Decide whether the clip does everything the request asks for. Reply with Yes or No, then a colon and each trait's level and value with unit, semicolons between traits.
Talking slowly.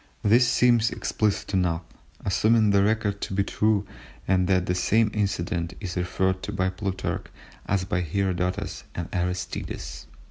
No: average, 145 wpm